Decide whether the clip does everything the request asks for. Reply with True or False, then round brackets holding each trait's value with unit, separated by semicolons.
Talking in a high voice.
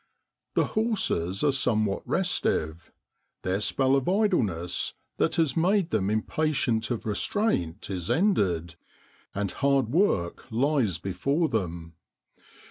False (115 Hz)